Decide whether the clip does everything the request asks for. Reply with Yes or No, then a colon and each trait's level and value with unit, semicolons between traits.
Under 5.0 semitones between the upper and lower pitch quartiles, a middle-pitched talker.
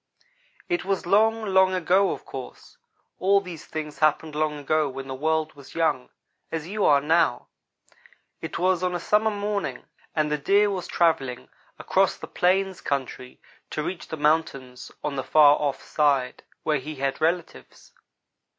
Yes: average, 4.5 semitones; medium, 160 Hz